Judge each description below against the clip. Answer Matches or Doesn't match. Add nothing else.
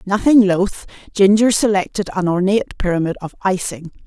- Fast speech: Doesn't match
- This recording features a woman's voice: Matches